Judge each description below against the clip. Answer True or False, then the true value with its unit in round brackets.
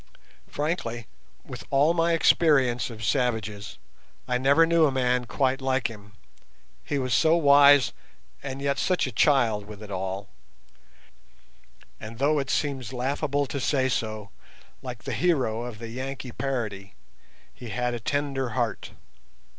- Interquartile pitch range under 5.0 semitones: True (3.7 semitones)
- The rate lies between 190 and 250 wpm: False (145 wpm)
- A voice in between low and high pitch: False (130 Hz)